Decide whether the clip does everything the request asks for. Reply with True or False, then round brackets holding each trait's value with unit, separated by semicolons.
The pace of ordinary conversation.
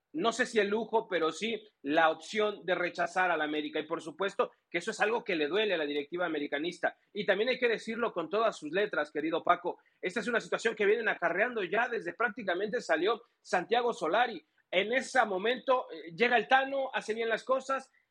False (205 wpm)